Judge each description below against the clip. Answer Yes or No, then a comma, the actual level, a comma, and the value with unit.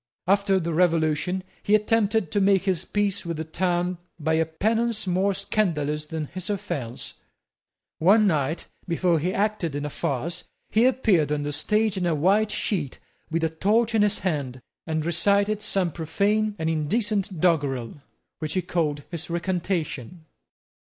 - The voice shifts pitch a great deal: No, average, 4.3 semitones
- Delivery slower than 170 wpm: Yes, average, 155 wpm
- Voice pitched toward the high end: No, medium, 175 Hz